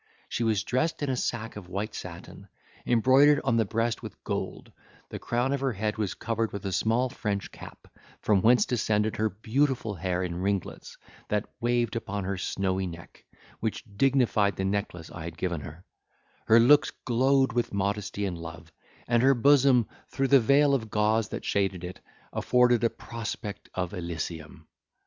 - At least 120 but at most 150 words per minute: No, average, 170 wpm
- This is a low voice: Yes, low, 110 Hz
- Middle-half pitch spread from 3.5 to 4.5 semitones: Yes, average, 4.2 semitones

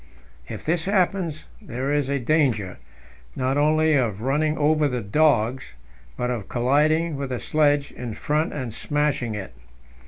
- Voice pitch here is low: No, medium, 145 Hz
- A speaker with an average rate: Yes, average, 150 wpm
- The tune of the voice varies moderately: Yes, average, 4.0 semitones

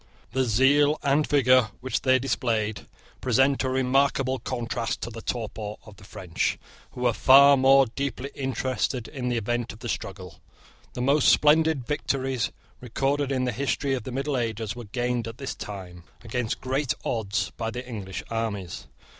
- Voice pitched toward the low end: Yes, low, 125 Hz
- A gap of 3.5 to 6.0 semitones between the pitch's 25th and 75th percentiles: No, average, 3.1 semitones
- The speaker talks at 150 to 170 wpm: Yes, average, 165 wpm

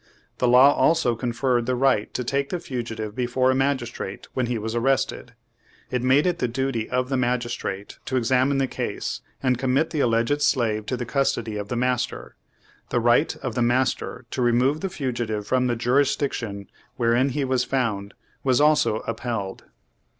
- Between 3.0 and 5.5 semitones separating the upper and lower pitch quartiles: No, narrow, 2.4 semitones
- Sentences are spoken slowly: No, average, 180 wpm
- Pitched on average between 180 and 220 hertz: No, low, 125 Hz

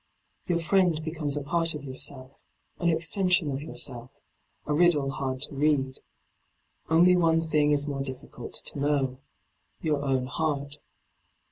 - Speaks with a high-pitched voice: No, medium, 150 Hz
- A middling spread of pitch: Yes, average, 3.0 semitones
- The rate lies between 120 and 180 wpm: Yes, average, 145 wpm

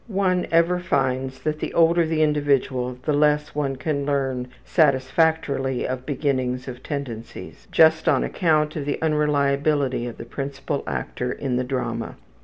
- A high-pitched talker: No, medium, 140 Hz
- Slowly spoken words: No, average, 150 wpm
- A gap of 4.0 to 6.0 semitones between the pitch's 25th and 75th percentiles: No, average, 3.1 semitones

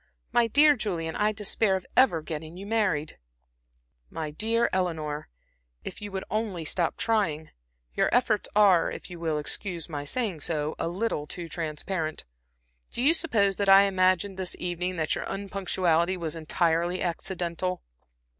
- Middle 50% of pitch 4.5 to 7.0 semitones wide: No, average, 3.8 semitones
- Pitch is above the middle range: No, medium, 180 Hz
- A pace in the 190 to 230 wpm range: No, average, 155 wpm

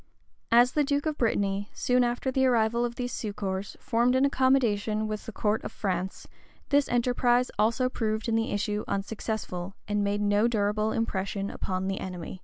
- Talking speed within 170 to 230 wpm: Yes, average, 175 wpm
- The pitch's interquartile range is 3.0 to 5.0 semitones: Yes, average, 3.3 semitones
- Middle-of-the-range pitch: No, high, 220 Hz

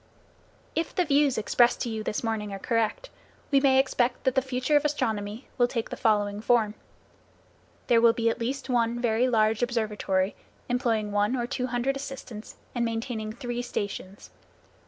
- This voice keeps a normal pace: Yes, average, 170 wpm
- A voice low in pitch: No, high, 235 Hz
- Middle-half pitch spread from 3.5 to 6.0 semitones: No, average, 2.9 semitones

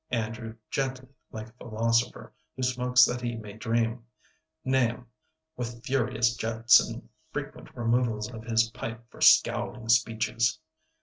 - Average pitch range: No, narrow, 1.5 semitones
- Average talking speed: No, slow, 130 wpm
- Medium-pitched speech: No, low, 115 Hz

